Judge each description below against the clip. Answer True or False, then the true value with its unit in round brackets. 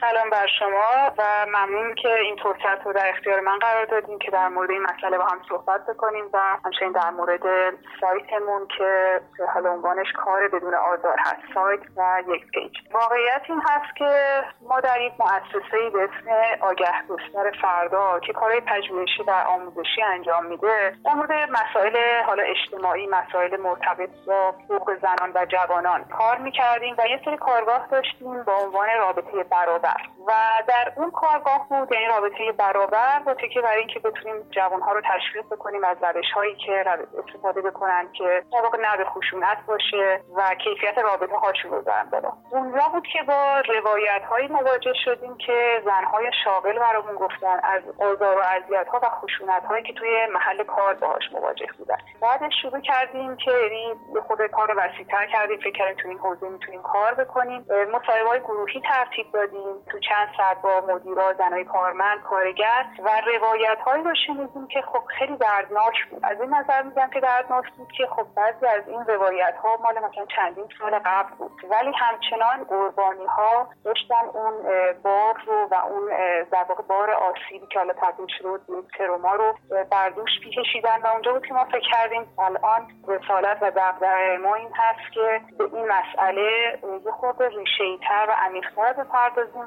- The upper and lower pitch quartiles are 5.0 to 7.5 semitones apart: False (4.0 semitones)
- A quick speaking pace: True (170 wpm)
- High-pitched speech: True (210 Hz)